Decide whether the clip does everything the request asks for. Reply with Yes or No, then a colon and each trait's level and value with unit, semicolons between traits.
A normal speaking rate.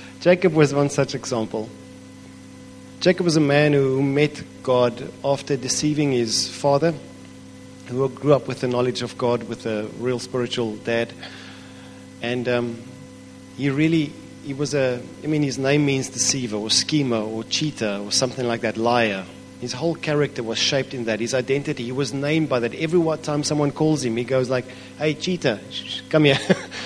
Yes: average, 165 wpm